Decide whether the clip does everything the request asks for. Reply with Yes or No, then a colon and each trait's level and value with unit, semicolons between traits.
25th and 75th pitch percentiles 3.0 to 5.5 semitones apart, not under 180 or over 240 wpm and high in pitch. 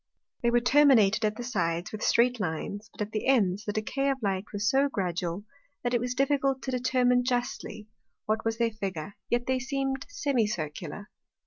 Yes: average, 4.0 semitones; average, 185 wpm; high, 230 Hz